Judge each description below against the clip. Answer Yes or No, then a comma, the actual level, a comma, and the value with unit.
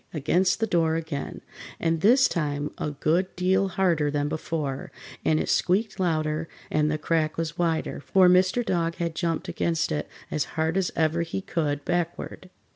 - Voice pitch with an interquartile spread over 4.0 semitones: No, average, 2.8 semitones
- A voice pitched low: No, medium, 165 Hz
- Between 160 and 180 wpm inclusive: Yes, average, 170 wpm